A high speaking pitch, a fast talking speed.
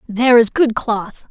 No: high, 230 Hz; average, 185 wpm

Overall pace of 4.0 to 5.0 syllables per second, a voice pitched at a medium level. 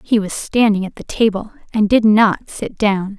No: 4.5 syllables/s; high, 210 Hz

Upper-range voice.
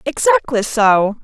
Yes: very high, 250 Hz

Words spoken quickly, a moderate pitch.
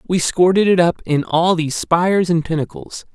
No: average, 190 wpm; medium, 170 Hz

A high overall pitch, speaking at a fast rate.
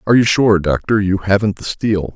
No: low, 100 Hz; fast, 225 wpm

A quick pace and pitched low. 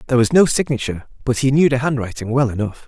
Yes: fast, 230 wpm; low, 125 Hz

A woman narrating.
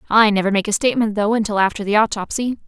Yes: female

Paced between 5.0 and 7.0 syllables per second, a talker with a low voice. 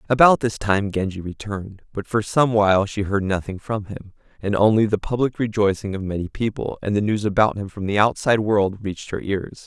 Yes: 5.5 syllables/s; low, 105 Hz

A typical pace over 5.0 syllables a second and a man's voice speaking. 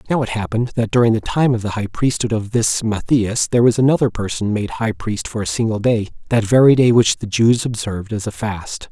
Yes: 5.5 syllables/s; male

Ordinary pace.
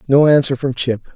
No: fast, 210 wpm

